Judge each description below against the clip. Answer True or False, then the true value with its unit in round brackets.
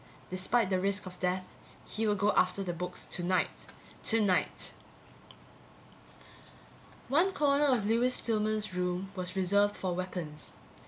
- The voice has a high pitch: True (195 Hz)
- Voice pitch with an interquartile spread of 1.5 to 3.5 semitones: True (3.0 semitones)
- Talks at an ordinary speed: False (125 wpm)